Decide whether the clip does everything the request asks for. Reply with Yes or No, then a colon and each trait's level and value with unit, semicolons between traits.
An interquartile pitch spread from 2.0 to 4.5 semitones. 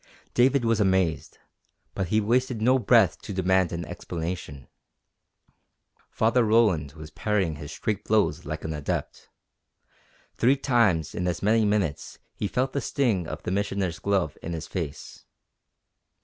No: average, 5.3 semitones